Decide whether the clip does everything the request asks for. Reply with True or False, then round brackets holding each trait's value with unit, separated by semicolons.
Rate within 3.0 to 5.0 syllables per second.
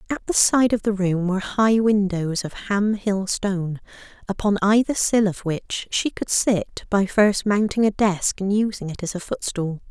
True (4.5 syllables/s)